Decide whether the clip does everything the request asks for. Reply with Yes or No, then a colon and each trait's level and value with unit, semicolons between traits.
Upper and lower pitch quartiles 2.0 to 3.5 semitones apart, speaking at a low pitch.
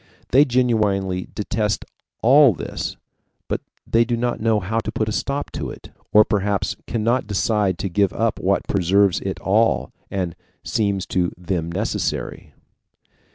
Yes: average, 3.1 semitones; low, 105 Hz